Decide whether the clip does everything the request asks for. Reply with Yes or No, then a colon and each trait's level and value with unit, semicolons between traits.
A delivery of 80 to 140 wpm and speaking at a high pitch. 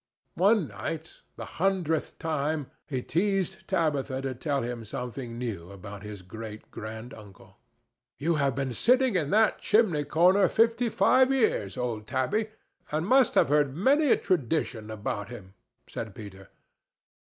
No: slow, 135 wpm; medium, 140 Hz